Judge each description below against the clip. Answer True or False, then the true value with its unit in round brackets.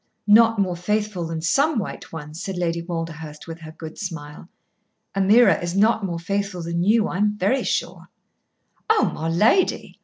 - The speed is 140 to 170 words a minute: True (160 wpm)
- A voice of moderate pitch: True (180 Hz)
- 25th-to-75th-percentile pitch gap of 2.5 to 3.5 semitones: False (4.1 semitones)